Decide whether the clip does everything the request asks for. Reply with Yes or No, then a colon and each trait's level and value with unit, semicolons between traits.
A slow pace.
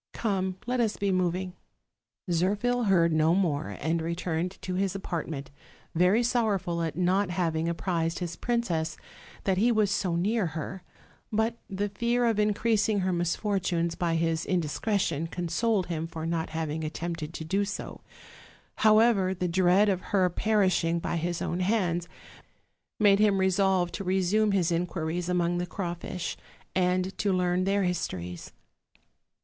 No: average, 150 wpm